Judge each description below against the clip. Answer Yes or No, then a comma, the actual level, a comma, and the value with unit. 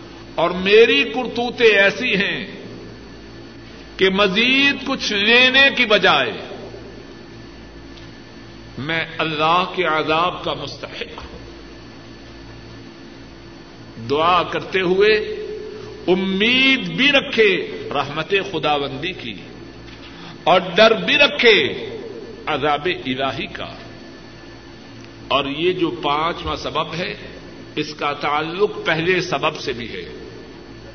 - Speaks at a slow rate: Yes, slow, 95 wpm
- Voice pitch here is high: Yes, high, 205 Hz